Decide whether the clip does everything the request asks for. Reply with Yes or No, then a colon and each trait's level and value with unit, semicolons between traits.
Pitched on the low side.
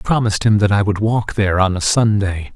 Yes: low, 100 Hz